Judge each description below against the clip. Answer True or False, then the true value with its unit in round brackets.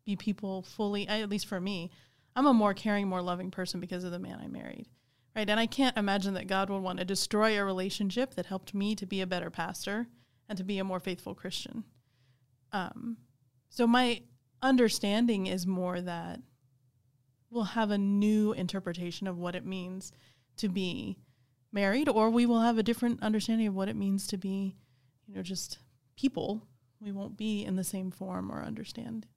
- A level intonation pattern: False (3.6 semitones)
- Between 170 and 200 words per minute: True (190 wpm)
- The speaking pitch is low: False (195 Hz)